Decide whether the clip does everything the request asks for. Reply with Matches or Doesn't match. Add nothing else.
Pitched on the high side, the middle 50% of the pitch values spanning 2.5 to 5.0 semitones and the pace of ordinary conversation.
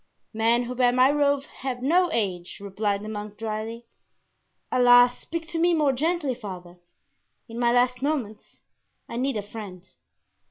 Matches